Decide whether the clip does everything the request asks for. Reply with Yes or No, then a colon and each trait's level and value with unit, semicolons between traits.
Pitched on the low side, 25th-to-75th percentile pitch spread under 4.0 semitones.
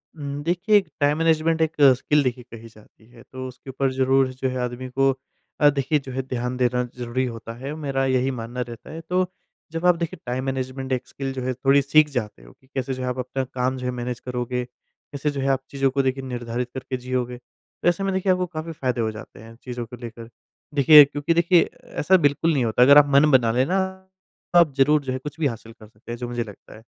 Yes: low, 130 Hz; average, 3.0 semitones